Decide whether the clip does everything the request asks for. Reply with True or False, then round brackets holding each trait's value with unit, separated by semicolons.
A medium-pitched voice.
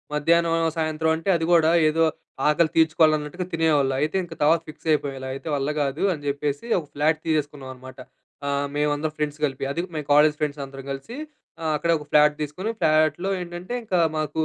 True (150 Hz)